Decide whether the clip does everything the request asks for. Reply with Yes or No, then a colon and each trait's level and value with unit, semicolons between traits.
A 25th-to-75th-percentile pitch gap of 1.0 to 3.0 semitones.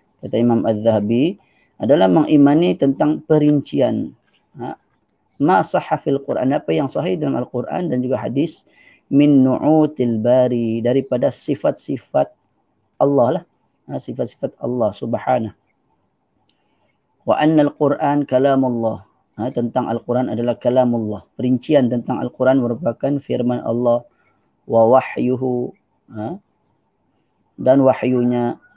Yes: narrow, 2.6 semitones